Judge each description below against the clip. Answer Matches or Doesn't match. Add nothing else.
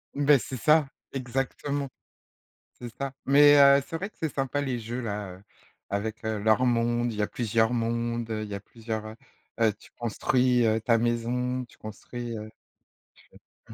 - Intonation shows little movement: Doesn't match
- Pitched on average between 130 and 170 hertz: Doesn't match